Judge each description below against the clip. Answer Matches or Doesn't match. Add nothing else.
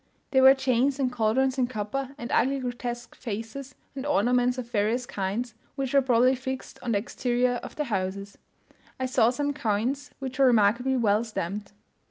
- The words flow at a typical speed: Matches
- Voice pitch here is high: Matches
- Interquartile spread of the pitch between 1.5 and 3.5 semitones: Matches